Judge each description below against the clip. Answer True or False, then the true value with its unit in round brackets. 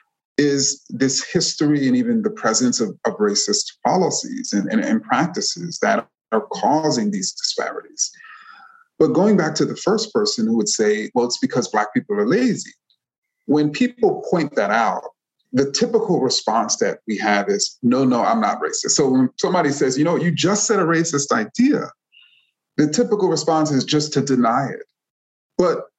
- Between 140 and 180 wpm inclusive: True (175 wpm)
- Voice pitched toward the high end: True (205 Hz)